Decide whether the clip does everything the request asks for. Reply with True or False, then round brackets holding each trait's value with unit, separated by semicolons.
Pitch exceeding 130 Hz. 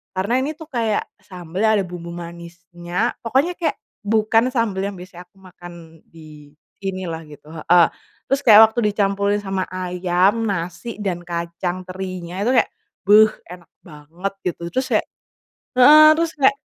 True (185 Hz)